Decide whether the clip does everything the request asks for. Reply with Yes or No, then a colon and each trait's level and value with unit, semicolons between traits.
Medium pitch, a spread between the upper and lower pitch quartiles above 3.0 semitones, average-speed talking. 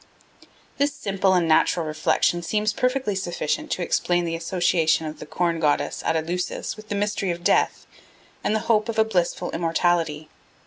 Yes: medium, 175 Hz; average, 4.1 semitones; average, 170 wpm